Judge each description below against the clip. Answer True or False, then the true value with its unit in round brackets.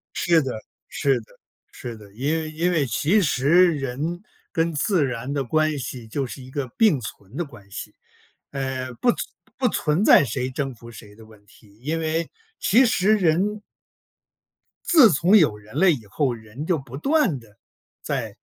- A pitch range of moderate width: False (5.8 semitones)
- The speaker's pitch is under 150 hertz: True (140 Hz)